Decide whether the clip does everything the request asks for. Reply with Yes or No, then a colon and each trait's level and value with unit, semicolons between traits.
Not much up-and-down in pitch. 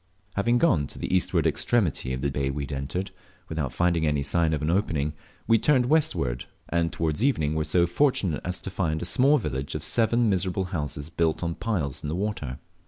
No: average, 5.1 semitones